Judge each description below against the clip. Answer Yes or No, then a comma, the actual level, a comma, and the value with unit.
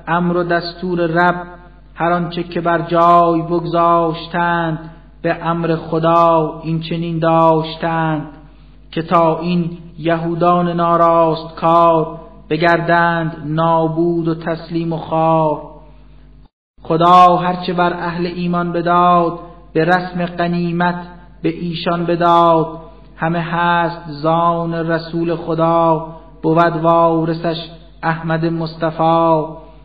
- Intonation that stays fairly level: Yes, narrow, 0.9 semitones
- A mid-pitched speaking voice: Yes, medium, 170 Hz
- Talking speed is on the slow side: Yes, slow, 100 wpm